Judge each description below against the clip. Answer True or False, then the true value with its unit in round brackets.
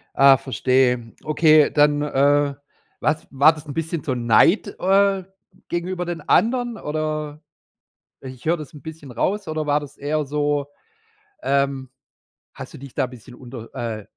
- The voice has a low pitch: False (145 Hz)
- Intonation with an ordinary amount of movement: True (3.0 semitones)